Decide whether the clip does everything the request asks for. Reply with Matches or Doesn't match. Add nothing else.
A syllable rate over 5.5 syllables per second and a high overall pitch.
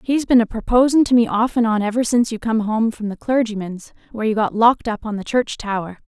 Matches